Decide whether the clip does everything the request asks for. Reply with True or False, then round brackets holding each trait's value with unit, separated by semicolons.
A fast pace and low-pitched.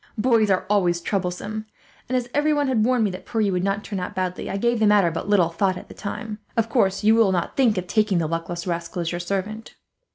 False (235 wpm; 200 Hz)